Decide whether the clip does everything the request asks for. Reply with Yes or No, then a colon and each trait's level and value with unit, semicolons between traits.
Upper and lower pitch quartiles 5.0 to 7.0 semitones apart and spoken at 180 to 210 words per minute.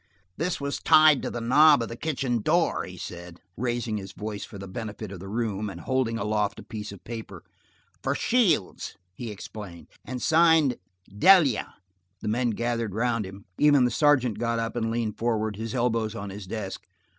No: average, 3.5 semitones; average, 185 wpm